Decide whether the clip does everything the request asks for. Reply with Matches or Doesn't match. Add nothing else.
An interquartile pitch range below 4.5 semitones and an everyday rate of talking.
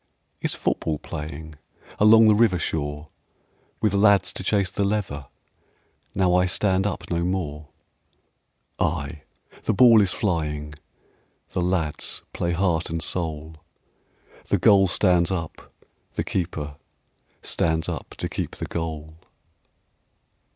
Doesn't match